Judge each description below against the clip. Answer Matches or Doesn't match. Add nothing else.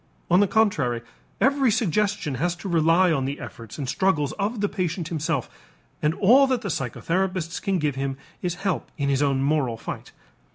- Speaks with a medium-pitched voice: Matches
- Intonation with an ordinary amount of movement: Doesn't match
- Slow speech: Doesn't match